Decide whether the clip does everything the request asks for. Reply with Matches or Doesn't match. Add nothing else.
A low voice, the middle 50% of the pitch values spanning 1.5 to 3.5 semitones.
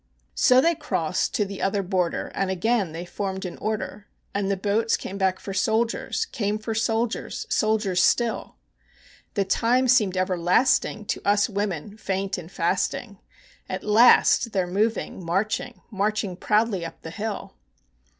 Doesn't match